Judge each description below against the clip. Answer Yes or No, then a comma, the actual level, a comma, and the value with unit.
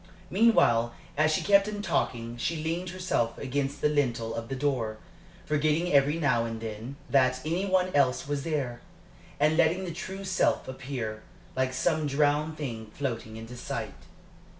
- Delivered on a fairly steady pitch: No, average, 5.3 semitones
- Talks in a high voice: No, medium, 140 Hz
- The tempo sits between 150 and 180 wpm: Yes, average, 160 wpm